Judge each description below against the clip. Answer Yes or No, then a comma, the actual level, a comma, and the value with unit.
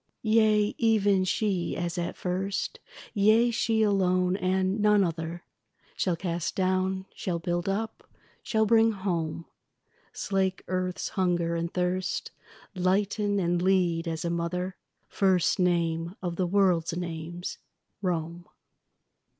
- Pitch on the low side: No, medium, 185 Hz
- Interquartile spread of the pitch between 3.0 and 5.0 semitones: No, narrow, 2.4 semitones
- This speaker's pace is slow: Yes, slow, 120 wpm